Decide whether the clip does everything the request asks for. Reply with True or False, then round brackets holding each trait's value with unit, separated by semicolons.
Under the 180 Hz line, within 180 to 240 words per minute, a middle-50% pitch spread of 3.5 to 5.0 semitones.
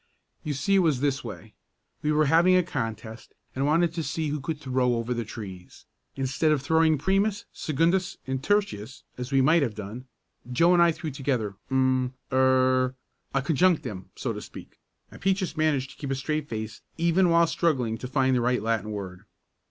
True (135 Hz; 190 wpm; 4.7 semitones)